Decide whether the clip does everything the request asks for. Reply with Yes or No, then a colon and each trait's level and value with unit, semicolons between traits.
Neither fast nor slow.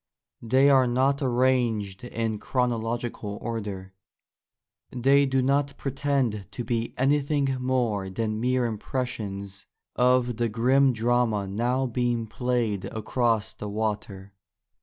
No: slow, 115 wpm